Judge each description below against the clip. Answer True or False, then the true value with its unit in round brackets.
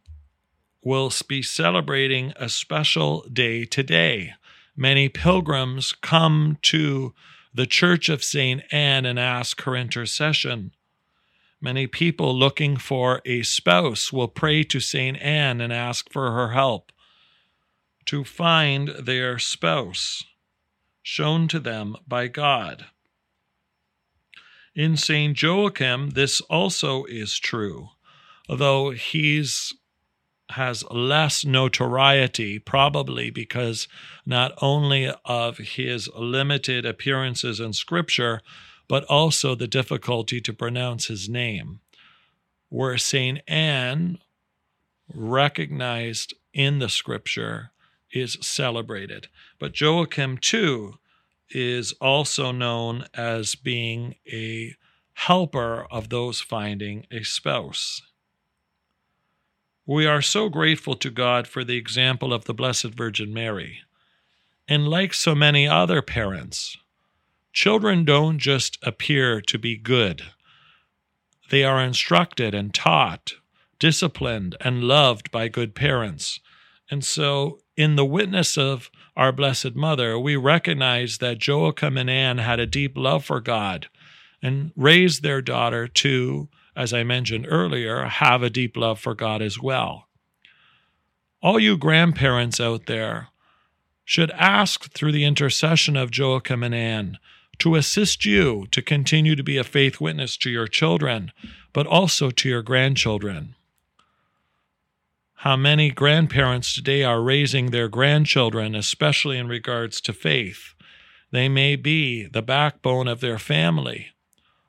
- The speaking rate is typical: False (120 wpm)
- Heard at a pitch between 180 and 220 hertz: False (130 Hz)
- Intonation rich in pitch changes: False (3.7 semitones)